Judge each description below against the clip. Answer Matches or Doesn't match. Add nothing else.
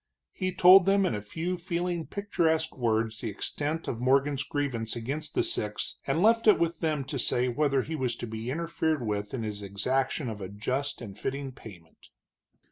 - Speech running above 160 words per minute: Matches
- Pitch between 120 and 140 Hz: Matches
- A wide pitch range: Matches